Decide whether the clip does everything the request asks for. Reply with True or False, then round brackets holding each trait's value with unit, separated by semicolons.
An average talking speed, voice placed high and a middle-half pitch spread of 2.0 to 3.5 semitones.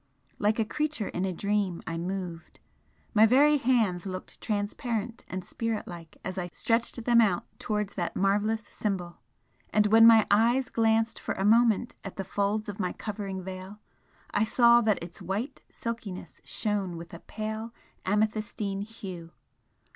True (155 wpm; 210 Hz; 3.1 semitones)